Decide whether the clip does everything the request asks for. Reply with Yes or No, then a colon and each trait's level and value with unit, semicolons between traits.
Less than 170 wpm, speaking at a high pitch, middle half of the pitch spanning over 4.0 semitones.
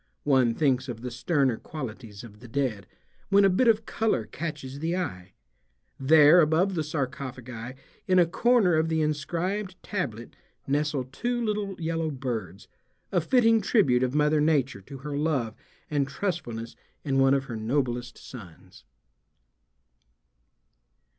No: average, 140 wpm; medium, 145 Hz; wide, 5.4 semitones